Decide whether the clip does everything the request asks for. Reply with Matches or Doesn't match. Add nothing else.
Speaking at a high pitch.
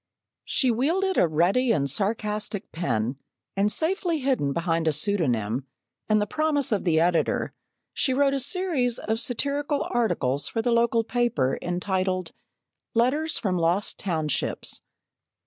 Matches